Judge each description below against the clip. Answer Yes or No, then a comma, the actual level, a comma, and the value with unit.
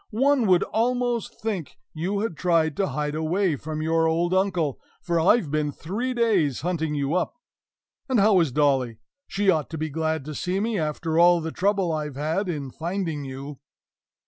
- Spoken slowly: No, average, 180 wpm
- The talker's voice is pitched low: No, medium, 165 Hz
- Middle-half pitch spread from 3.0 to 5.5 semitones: Yes, average, 4.4 semitones